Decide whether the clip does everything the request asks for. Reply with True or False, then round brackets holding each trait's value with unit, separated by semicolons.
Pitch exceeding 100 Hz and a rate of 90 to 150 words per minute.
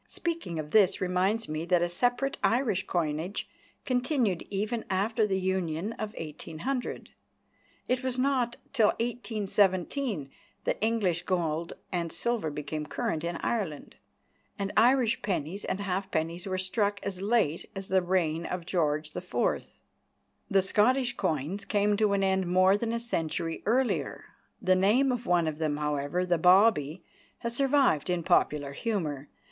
True (190 Hz; 145 wpm)